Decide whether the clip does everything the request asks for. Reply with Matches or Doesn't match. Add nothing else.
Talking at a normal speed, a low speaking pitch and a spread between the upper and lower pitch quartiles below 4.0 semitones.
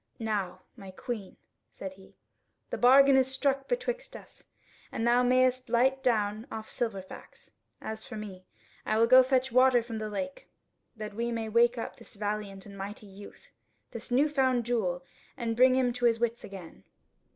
Doesn't match